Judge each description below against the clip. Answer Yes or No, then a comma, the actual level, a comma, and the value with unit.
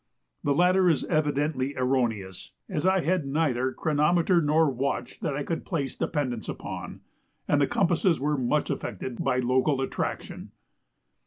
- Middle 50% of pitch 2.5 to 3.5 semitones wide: No, average, 4.0 semitones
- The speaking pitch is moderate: Yes, medium, 145 Hz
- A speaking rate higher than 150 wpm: No, average, 145 wpm